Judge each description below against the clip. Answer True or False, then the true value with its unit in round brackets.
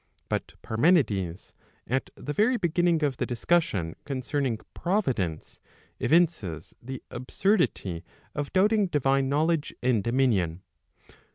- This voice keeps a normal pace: False (105 wpm)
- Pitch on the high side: False (135 Hz)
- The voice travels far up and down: True (7.5 semitones)